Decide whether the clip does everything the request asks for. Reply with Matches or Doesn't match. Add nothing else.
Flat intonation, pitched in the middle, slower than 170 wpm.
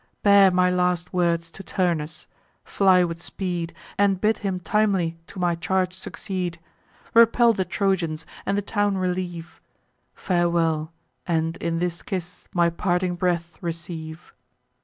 Matches